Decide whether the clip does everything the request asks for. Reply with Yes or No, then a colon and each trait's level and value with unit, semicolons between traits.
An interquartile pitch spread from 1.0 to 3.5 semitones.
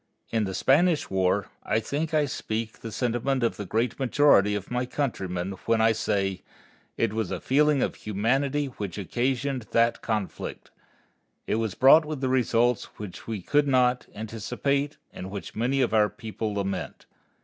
No: average, 4.3 semitones